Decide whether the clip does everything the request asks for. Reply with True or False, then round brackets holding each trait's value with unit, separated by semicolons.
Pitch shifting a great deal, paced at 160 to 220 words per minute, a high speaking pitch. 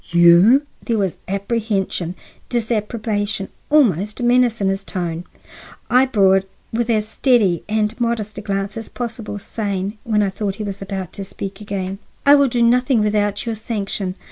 False (3.1 semitones; 165 wpm; 210 Hz)